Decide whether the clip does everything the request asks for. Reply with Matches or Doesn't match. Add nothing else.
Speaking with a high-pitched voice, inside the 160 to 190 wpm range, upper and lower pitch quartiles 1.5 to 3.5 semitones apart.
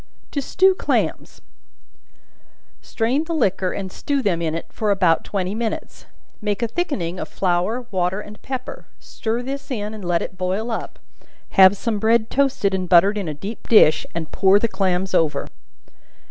Doesn't match